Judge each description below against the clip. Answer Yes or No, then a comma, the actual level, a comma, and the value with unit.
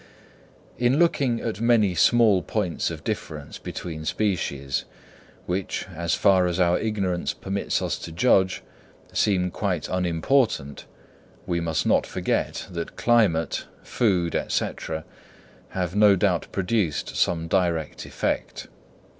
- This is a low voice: Yes, very low, 90 Hz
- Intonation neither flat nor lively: Yes, average, 4.2 semitones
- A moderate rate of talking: No, slow, 120 wpm